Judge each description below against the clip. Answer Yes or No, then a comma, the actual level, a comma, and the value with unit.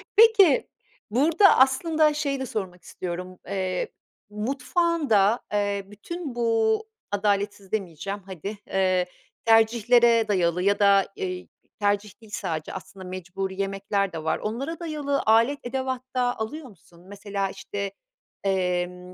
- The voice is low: No, high, 205 Hz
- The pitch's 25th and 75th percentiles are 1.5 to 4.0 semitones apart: No, average, 5.0 semitones